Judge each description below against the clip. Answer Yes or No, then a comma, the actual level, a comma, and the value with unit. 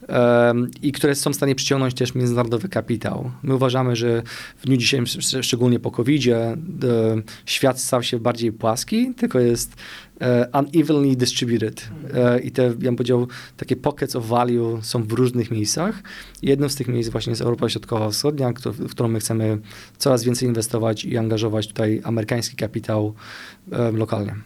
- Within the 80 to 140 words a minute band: No, average, 150 wpm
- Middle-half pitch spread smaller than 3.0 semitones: Yes, narrow, 2.5 semitones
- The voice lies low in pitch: Yes, low, 120 Hz